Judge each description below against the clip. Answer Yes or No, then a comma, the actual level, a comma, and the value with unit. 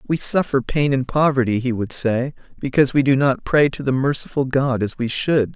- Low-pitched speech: Yes, low, 130 Hz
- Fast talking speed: Yes, fast, 215 wpm